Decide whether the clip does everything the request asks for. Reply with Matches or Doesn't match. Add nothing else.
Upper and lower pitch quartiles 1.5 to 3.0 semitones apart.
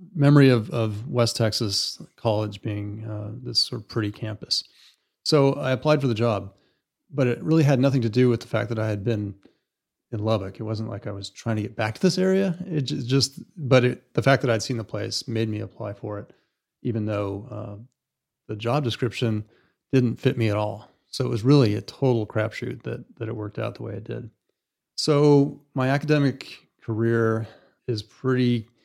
Doesn't match